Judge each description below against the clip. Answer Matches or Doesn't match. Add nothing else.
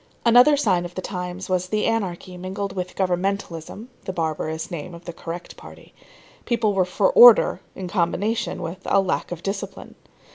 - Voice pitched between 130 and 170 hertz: Doesn't match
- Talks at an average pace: Matches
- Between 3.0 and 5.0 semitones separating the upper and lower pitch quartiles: Doesn't match